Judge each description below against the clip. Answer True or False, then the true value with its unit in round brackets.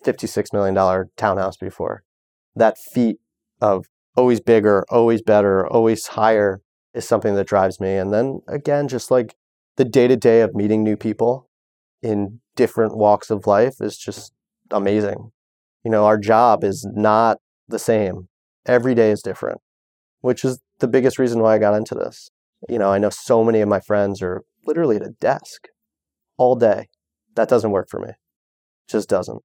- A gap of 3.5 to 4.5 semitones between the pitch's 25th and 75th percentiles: False (3.0 semitones)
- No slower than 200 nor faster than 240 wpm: False (170 wpm)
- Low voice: True (105 Hz)